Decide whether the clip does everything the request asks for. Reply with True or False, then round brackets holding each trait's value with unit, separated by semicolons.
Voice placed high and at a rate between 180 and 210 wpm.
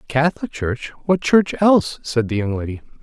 False (135 Hz; 200 wpm)